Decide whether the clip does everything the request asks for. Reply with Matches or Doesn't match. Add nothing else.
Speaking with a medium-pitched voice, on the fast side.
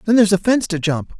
Doesn't match